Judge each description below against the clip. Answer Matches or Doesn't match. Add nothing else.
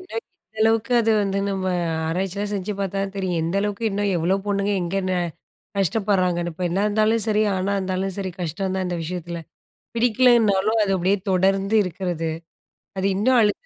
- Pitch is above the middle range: Matches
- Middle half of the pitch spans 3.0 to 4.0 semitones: Doesn't match